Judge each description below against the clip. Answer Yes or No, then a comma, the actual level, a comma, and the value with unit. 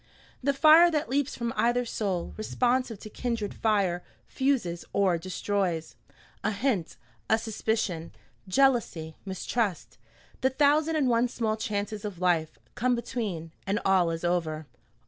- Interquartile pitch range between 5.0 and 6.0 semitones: Yes, wide, 5.5 semitones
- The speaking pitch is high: Yes, high, 215 Hz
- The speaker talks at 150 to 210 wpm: No, slow, 135 wpm